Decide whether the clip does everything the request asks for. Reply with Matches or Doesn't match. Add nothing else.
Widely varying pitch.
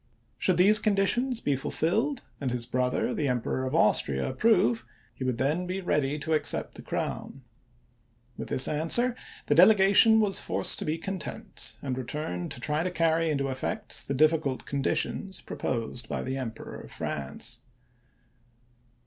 Matches